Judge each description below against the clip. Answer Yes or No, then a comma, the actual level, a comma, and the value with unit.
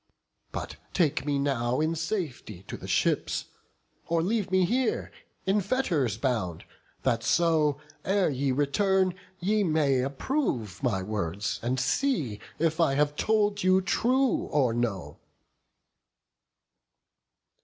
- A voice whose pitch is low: No, medium, 150 Hz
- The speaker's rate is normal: No, slow, 120 wpm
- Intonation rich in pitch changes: Yes, wide, 7.2 semitones